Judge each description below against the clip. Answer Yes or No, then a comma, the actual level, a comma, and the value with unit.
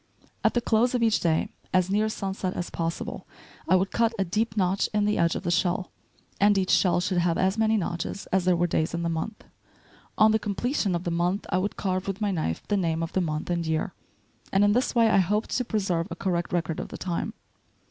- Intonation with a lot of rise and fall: No, average, 3.4 semitones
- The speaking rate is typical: No, fast, 240 wpm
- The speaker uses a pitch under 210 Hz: Yes, medium, 185 Hz